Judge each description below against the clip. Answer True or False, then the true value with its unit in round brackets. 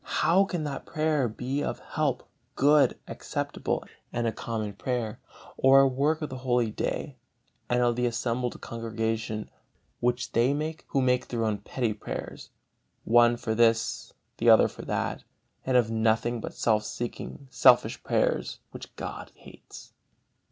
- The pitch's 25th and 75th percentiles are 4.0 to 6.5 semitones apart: False (3.1 semitones)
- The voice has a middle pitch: False (120 Hz)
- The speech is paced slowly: False (150 wpm)